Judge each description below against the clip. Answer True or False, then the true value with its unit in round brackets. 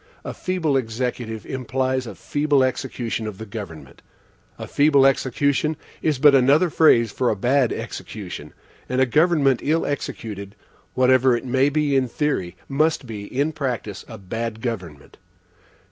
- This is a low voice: True (130 Hz)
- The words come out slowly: False (145 wpm)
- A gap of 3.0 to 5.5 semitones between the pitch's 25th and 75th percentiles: True (4.1 semitones)